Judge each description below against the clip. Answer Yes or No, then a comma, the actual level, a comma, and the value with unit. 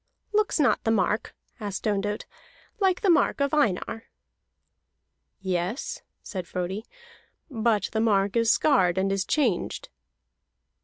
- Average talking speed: No, slow, 120 wpm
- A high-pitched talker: Yes, high, 215 Hz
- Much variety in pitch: Yes, wide, 6.0 semitones